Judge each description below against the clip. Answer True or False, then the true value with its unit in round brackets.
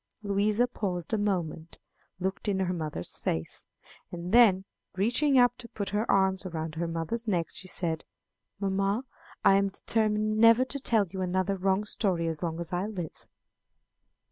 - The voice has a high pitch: True (195 Hz)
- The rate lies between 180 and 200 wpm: False (165 wpm)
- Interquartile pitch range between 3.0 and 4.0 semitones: True (3.5 semitones)